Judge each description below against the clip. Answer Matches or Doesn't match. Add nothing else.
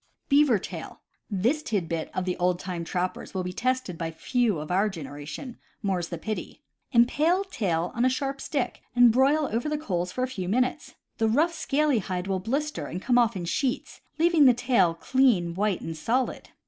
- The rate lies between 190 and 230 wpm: Matches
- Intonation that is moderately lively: Doesn't match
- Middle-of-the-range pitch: Doesn't match